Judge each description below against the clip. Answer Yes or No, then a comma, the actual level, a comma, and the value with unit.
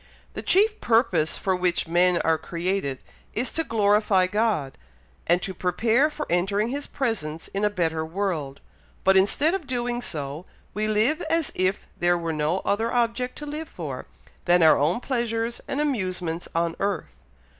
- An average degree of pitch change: No, wide, 5.7 semitones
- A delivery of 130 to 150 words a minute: No, average, 165 wpm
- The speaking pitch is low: No, high, 195 Hz